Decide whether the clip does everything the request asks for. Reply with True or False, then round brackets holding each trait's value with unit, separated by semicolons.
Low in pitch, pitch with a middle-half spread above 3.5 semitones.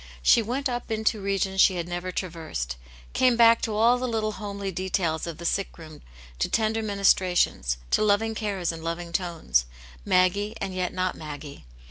False (190 Hz; 4.3 semitones)